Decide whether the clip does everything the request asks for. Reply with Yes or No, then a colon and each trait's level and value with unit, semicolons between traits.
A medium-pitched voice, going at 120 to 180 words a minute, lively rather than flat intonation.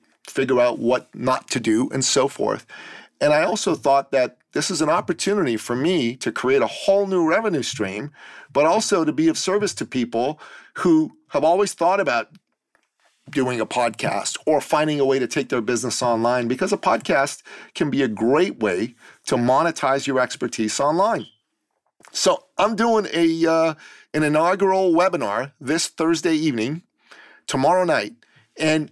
Yes: medium, 160 Hz; average, 165 wpm; wide, 6.4 semitones